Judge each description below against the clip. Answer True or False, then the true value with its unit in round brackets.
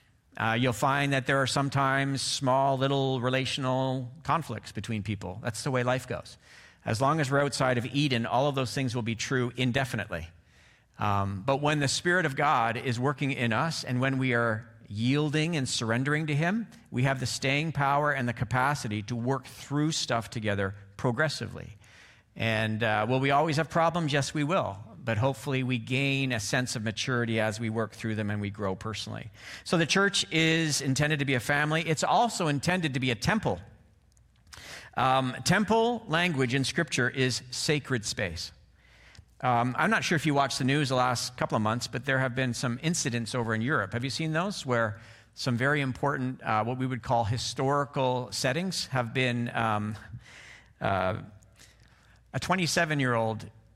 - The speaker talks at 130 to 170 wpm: False (185 wpm)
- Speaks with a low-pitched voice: True (130 Hz)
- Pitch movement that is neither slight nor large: True (3.8 semitones)